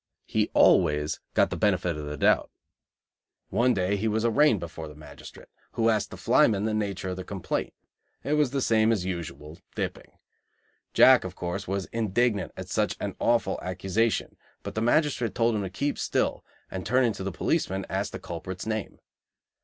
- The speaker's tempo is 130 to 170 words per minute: No, average, 180 wpm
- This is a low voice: Yes, low, 100 Hz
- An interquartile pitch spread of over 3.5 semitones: Yes, average, 4.0 semitones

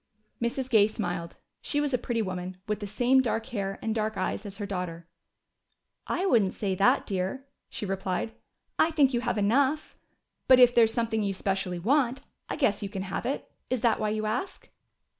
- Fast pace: No, average, 195 wpm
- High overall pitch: Yes, high, 215 Hz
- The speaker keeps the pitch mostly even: No, average, 4.3 semitones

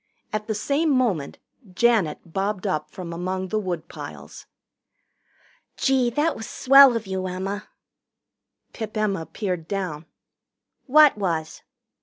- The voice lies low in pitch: No, high, 200 Hz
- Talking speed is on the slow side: Yes, slow, 120 wpm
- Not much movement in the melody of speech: No, average, 4.7 semitones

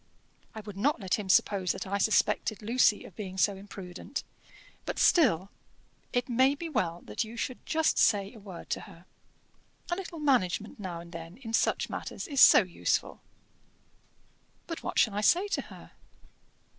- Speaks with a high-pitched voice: Yes, high, 210 Hz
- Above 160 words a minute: Yes, average, 170 wpm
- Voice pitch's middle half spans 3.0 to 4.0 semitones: No, average, 5.3 semitones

